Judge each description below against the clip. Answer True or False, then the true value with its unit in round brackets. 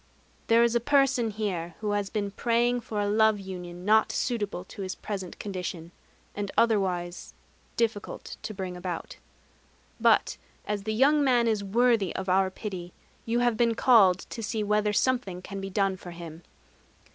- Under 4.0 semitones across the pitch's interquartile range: True (3.5 semitones)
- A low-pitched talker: False (205 Hz)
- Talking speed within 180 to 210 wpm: False (170 wpm)